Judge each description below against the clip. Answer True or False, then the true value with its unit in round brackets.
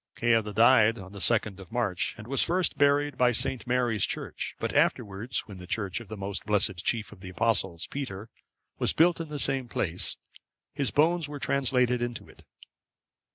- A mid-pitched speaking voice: False (115 Hz)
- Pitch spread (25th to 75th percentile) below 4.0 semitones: False (5.1 semitones)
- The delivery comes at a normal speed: True (185 wpm)